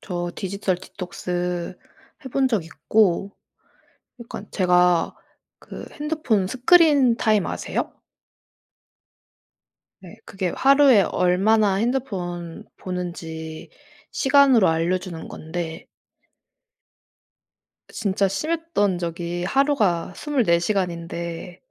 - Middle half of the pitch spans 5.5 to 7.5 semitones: No, average, 5.1 semitones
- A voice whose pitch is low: No, high, 190 Hz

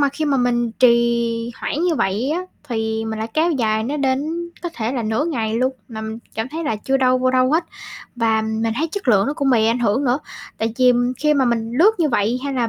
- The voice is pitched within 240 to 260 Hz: Yes, high, 245 Hz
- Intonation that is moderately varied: Yes, average, 4.0 semitones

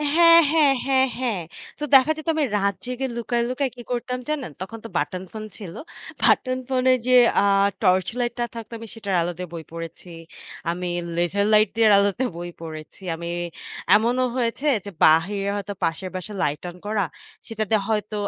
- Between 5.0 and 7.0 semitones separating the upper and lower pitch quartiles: Yes, wide, 5.5 semitones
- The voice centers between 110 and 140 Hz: No, high, 215 Hz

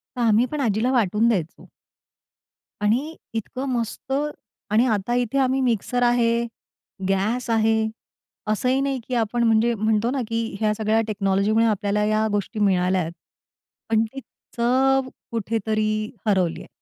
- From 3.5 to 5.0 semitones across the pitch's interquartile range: No, narrow, 2.4 semitones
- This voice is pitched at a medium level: No, high, 225 Hz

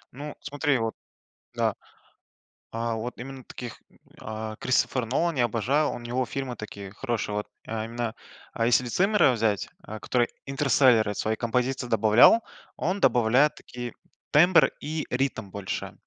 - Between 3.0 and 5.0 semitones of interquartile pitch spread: Yes, average, 3.5 semitones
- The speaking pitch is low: Yes, low, 120 Hz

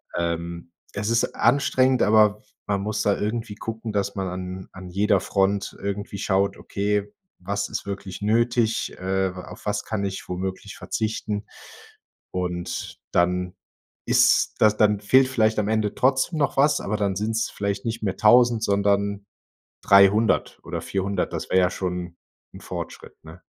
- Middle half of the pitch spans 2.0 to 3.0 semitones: Yes, narrow, 2.4 semitones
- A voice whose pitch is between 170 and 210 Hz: No, low, 100 Hz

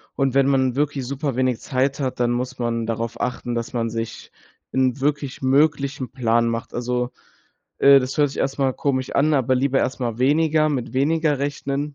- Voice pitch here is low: Yes, low, 130 Hz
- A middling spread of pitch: No, narrow, 2.3 semitones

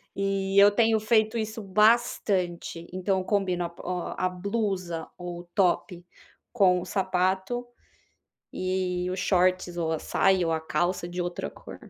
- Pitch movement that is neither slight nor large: No, narrow, 2.3 semitones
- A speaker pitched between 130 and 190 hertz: Yes, medium, 185 Hz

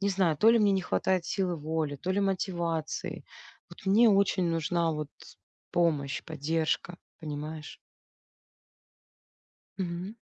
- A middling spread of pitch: Yes, average, 3.4 semitones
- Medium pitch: Yes, medium, 170 Hz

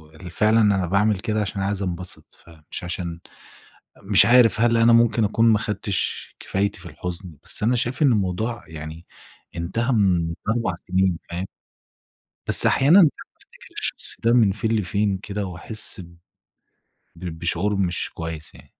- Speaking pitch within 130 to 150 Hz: No, low, 100 Hz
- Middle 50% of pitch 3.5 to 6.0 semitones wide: Yes, average, 4.1 semitones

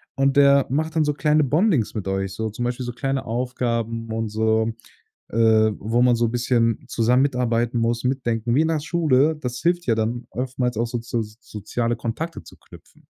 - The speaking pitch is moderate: No, low, 120 Hz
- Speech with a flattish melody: No, average, 3.1 semitones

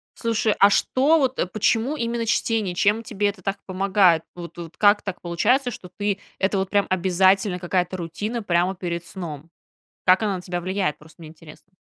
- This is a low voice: No, high, 190 Hz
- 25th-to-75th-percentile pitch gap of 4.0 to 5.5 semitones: No, average, 3.2 semitones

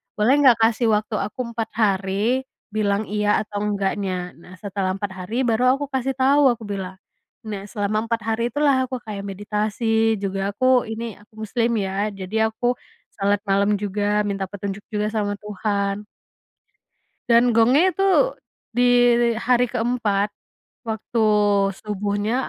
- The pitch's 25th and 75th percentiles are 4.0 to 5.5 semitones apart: No, average, 2.7 semitones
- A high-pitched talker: Yes, high, 215 Hz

